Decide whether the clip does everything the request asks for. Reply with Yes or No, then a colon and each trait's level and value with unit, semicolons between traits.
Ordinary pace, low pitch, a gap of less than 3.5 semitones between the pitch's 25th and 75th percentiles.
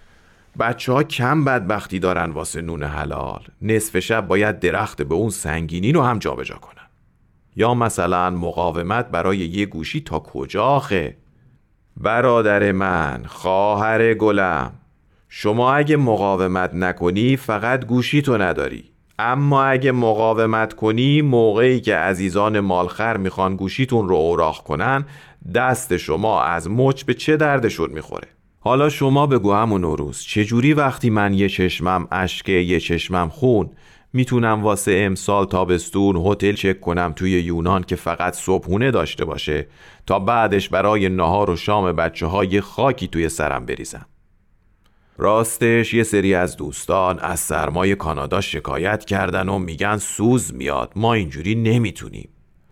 No: average, 135 wpm; low, 100 Hz; average, 4.3 semitones